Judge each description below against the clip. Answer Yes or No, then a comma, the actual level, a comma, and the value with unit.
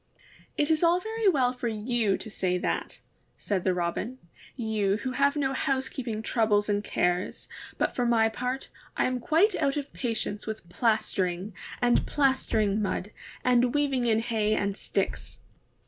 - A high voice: Yes, high, 235 Hz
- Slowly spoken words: No, average, 165 wpm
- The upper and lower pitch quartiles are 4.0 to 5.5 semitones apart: Yes, average, 4.3 semitones